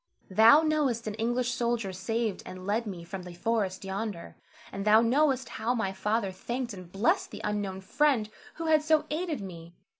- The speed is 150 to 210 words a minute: Yes, average, 180 wpm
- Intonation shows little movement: No, average, 4.3 semitones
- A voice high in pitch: Yes, high, 220 Hz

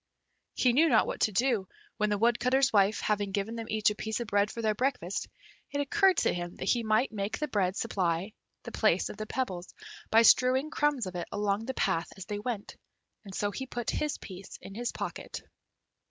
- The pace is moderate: No, fast, 210 wpm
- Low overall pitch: No, high, 215 Hz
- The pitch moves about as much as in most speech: Yes, average, 4.1 semitones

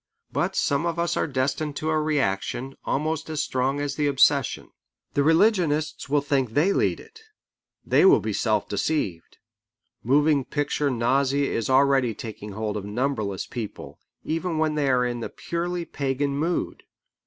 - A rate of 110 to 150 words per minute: No, average, 160 wpm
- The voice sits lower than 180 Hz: Yes, medium, 140 Hz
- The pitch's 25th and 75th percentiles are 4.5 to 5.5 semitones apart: No, average, 3.4 semitones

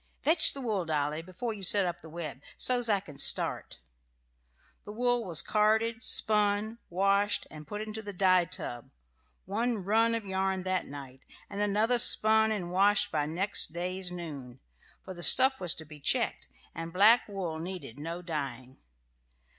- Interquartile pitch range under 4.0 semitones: No, average, 4.6 semitones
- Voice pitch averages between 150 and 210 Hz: Yes, high, 190 Hz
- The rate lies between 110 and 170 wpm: Yes, average, 165 wpm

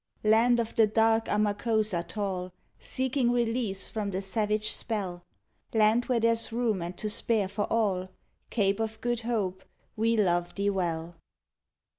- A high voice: Yes, high, 215 Hz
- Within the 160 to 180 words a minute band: No, average, 145 wpm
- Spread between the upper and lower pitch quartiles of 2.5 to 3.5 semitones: Yes, average, 3.0 semitones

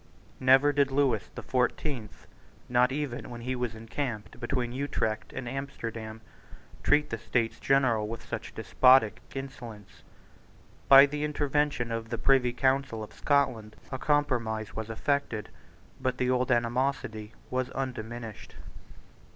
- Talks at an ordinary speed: No, slow, 130 wpm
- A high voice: No, low, 125 Hz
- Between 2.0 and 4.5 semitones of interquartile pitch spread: Yes, average, 3.2 semitones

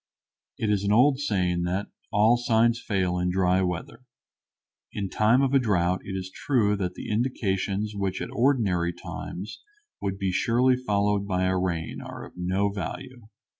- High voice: No, low, 100 Hz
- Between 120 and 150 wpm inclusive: No, average, 170 wpm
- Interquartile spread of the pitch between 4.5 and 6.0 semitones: No, average, 3.6 semitones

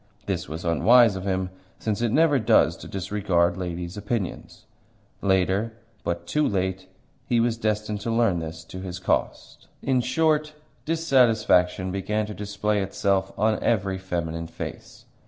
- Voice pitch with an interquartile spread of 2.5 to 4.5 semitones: Yes, average, 3.8 semitones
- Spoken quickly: No, average, 145 wpm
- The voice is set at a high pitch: No, low, 100 Hz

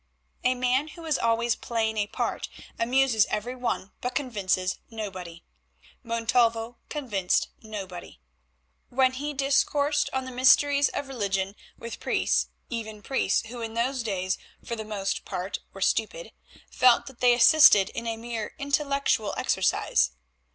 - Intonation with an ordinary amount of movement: Yes, average, 3.9 semitones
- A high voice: Yes, high, 235 Hz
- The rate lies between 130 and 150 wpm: Yes, average, 140 wpm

